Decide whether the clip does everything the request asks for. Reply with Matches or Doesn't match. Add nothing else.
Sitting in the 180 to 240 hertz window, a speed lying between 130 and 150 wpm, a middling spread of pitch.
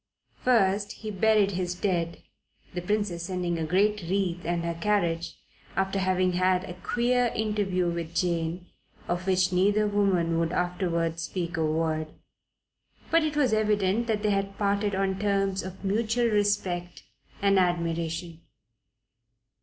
Matches